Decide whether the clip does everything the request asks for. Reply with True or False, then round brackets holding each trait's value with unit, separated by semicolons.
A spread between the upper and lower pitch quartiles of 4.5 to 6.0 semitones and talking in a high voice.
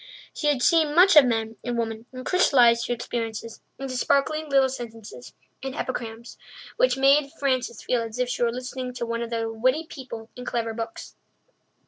False (3.0 semitones; 245 Hz)